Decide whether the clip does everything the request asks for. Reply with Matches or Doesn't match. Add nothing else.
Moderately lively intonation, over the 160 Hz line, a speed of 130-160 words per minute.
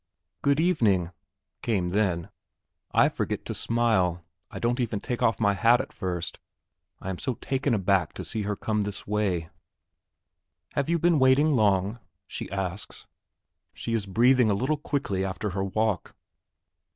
Doesn't match